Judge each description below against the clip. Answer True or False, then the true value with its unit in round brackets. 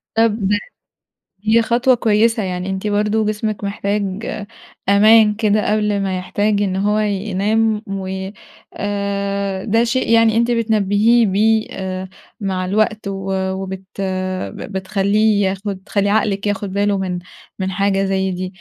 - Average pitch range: False (2.0 semitones)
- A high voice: True (205 Hz)